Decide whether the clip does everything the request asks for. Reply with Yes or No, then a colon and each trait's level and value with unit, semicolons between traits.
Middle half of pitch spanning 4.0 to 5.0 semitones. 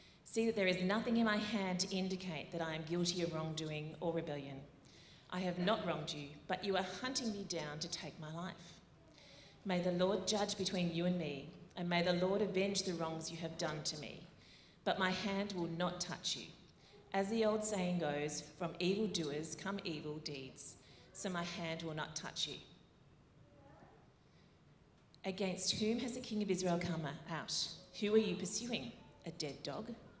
No: average, 3.4 semitones